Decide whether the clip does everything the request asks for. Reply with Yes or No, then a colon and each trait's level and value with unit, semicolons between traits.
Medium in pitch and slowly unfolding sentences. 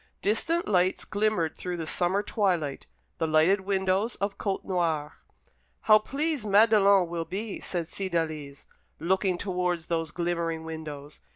Yes: medium, 180 Hz; slow, 125 wpm